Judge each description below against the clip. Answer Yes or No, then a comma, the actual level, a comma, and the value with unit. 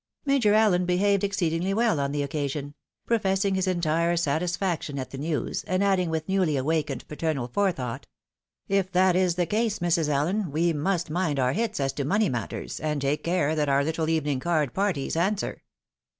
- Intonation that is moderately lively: Yes, average, 4.6 semitones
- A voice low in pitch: No, medium, 170 Hz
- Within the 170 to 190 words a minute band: Yes, average, 185 wpm